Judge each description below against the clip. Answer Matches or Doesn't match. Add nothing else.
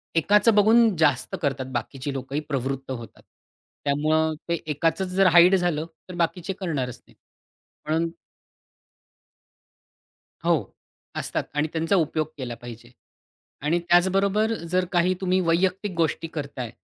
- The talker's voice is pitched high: Doesn't match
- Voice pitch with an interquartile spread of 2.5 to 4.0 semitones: Doesn't match